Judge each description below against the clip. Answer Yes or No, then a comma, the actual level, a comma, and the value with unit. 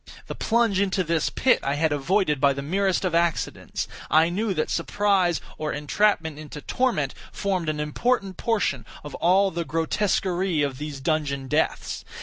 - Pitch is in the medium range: Yes, medium, 170 Hz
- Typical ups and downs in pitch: Yes, average, 4.7 semitones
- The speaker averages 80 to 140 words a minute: No, average, 160 wpm